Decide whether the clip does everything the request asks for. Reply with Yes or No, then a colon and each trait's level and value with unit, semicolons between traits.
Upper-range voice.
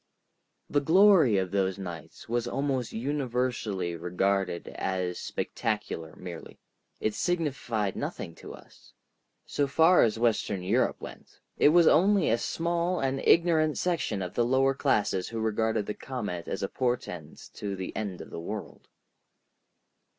No: low, 115 Hz